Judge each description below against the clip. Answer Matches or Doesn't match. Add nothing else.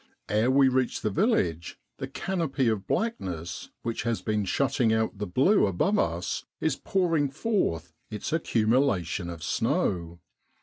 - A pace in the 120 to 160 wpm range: Matches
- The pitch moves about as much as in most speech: Doesn't match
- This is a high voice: Doesn't match